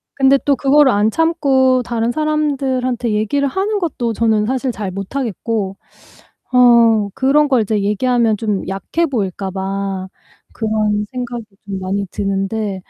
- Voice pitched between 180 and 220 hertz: No, high, 230 Hz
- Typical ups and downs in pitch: Yes, average, 4.7 semitones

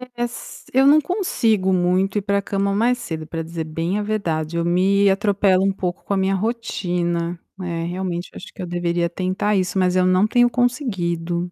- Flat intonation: No, average, 3.1 semitones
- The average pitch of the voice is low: No, medium, 185 Hz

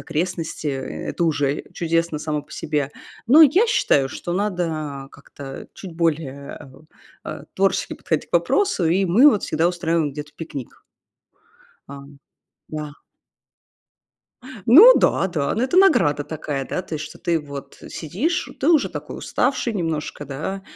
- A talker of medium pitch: Yes, medium, 165 Hz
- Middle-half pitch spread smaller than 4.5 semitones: No, average, 4.9 semitones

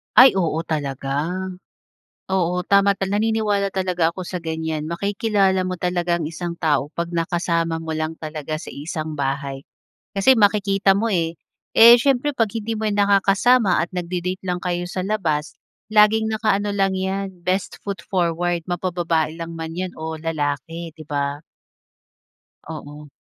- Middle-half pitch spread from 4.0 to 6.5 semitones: No, average, 3.6 semitones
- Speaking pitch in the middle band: Yes, medium, 175 Hz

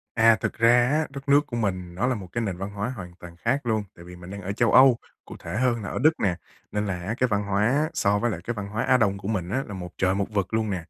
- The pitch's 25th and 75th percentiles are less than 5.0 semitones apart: Yes, average, 3.9 semitones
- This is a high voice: No, low, 105 Hz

